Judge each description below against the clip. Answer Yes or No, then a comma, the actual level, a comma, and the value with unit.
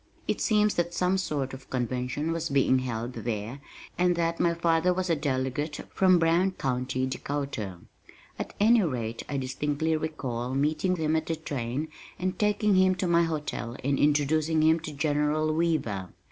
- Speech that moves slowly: No, average, 165 wpm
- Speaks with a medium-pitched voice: Yes, medium, 155 Hz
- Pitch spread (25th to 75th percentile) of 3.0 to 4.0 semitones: No, average, 4.5 semitones